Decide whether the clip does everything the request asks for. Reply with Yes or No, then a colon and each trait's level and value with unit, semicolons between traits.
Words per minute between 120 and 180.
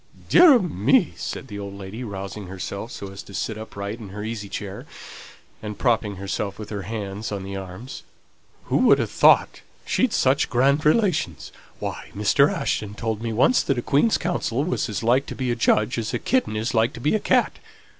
No: fast, 205 wpm